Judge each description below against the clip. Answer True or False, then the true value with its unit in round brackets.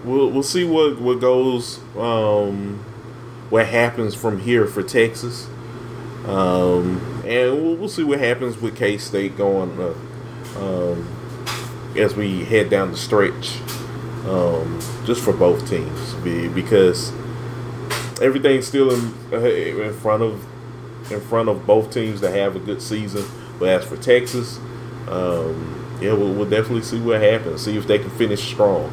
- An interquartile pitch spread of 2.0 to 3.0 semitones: True (2.6 semitones)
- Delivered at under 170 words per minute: True (150 wpm)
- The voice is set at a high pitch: False (120 Hz)